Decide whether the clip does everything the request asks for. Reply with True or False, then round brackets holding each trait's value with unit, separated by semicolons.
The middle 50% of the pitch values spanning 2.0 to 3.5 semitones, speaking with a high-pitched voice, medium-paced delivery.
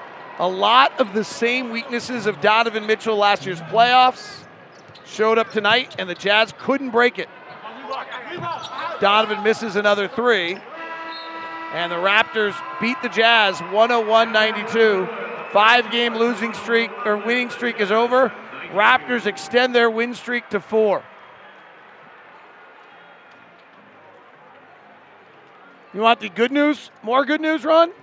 False (2.6 semitones; 230 Hz; 125 wpm)